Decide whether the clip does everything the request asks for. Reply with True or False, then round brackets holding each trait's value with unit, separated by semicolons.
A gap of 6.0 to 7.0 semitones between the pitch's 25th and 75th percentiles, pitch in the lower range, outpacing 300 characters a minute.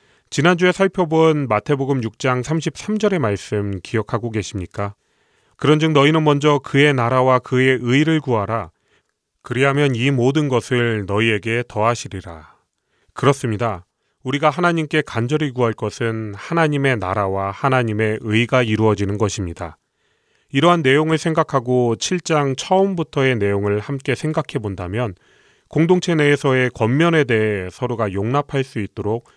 False (5.4 semitones; 130 Hz; 310 characters per minute)